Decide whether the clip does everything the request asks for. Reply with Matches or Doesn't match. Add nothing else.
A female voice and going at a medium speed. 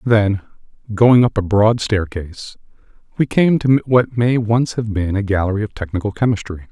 Doesn't match